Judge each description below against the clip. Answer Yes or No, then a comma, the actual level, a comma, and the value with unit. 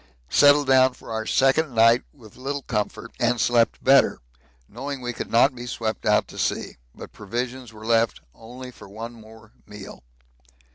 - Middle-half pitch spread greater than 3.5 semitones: No, narrow, 2.6 semitones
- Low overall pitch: Yes, low, 120 Hz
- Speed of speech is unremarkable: Yes, average, 170 wpm